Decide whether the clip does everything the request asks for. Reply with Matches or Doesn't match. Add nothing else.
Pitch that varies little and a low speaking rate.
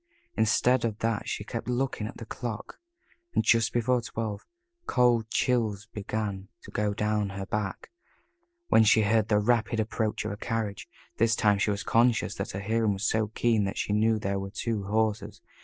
Doesn't match